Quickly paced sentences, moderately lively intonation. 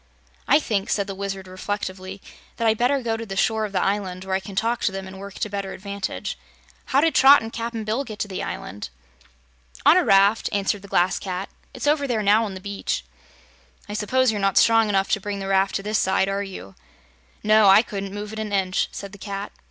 No: fast, 230 wpm; narrow, 2.2 semitones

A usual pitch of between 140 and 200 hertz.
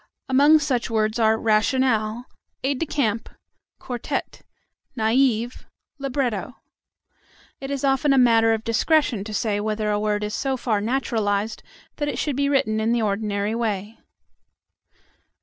No: high, 230 Hz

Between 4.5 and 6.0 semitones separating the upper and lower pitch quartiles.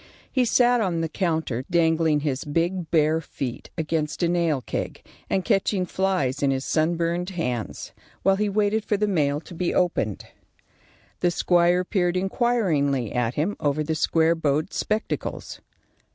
No: average, 4.0 semitones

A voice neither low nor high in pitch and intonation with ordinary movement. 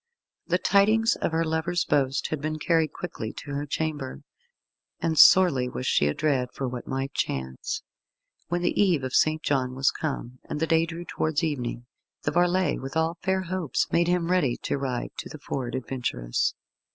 Yes: medium, 155 Hz; average, 4.4 semitones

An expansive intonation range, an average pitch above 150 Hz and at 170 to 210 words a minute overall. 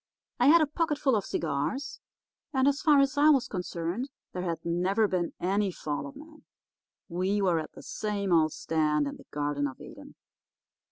Yes: wide, 8.7 semitones; high, 190 Hz; average, 180 wpm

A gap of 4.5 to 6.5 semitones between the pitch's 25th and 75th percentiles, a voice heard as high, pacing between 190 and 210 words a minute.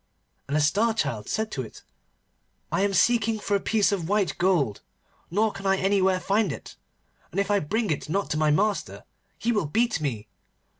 Yes: wide, 5.5 semitones; high, 195 Hz; average, 195 wpm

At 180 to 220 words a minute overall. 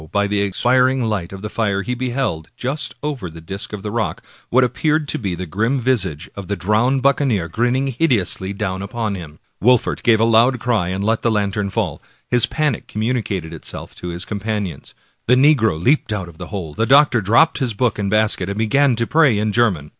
Yes: fast, 205 wpm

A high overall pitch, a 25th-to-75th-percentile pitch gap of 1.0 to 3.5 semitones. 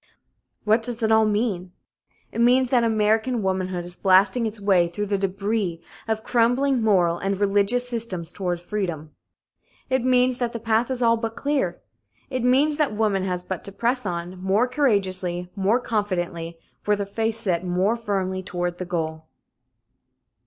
No: high, 205 Hz; average, 4.1 semitones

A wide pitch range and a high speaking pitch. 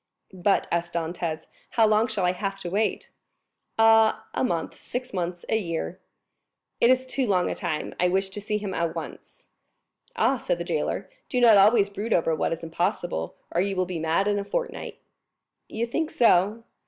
No: average, 4.2 semitones; high, 195 Hz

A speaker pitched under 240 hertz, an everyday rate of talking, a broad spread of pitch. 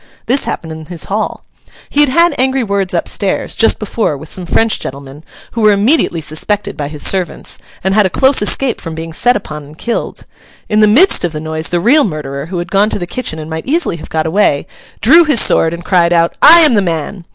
No: high, 190 Hz; fast, 230 wpm; wide, 6.1 semitones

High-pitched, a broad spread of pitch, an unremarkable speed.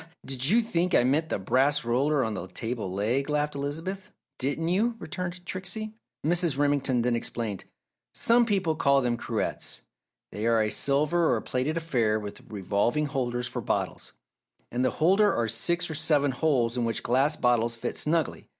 No: medium, 140 Hz; wide, 5.7 semitones; average, 180 wpm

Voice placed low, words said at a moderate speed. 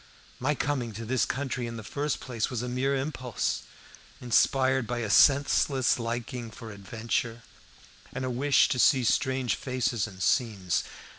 Yes: low, 125 Hz; average, 155 wpm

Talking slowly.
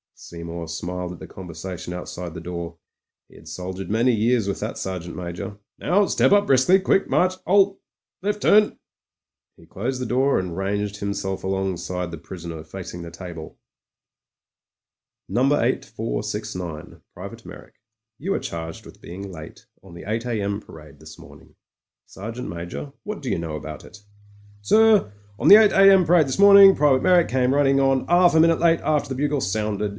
No: average, 170 wpm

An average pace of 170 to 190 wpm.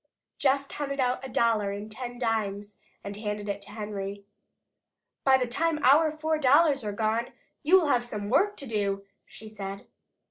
Yes: average, 175 wpm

